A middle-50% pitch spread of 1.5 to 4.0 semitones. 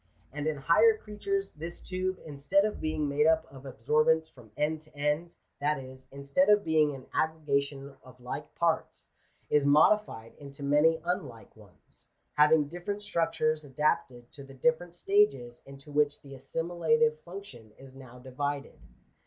Yes: average, 3.6 semitones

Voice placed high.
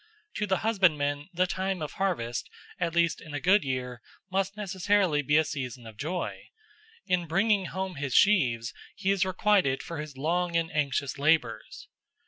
No: medium, 170 Hz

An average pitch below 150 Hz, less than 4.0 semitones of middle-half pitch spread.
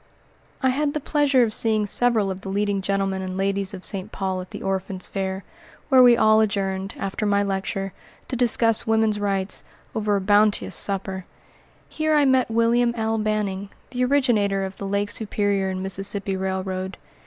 No: high, 200 Hz; narrow, 2.6 semitones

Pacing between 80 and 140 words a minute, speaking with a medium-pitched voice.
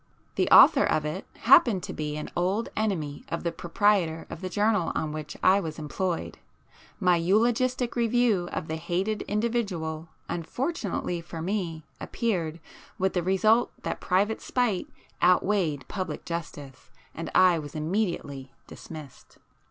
Yes: slow, 135 wpm; medium, 180 Hz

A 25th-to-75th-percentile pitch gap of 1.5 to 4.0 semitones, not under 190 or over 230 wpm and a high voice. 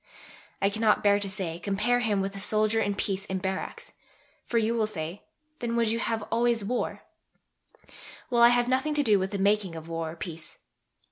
Yes: average, 3.3 semitones; average, 200 wpm; high, 205 Hz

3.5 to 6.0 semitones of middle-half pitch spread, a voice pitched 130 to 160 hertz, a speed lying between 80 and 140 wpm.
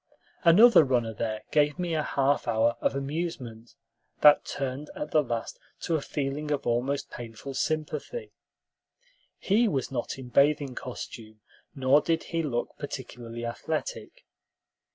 Yes: average, 4.5 semitones; medium, 140 Hz; slow, 135 wpm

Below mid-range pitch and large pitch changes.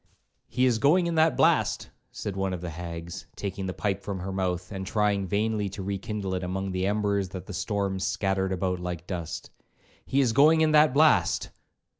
No: very low, 95 Hz; average, 2.7 semitones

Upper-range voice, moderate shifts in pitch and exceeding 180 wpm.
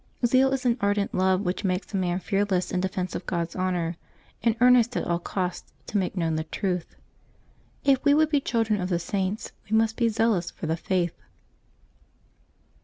Yes: high, 195 Hz; average, 4.1 semitones; average, 190 wpm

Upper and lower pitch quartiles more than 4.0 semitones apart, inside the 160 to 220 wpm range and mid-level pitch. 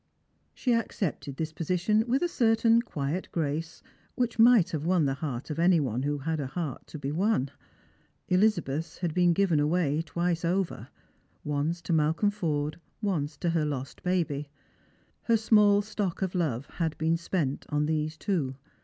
Yes: average, 4.5 semitones; average, 165 wpm; medium, 165 Hz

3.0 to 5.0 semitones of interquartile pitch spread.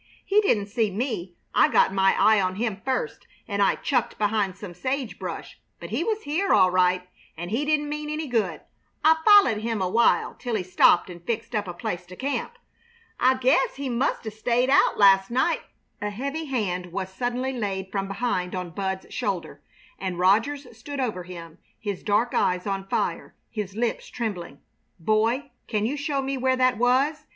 No: wide, 5.4 semitones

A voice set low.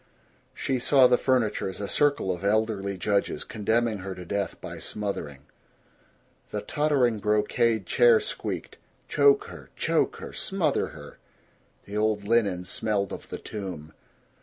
Yes: low, 105 Hz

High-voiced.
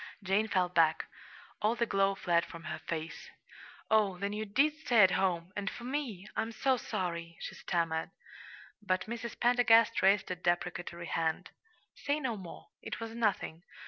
Yes: high, 195 Hz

